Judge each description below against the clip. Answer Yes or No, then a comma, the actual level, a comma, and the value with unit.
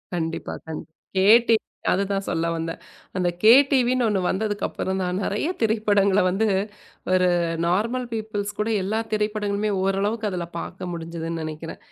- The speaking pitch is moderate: No, high, 200 Hz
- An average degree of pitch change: Yes, average, 3.3 semitones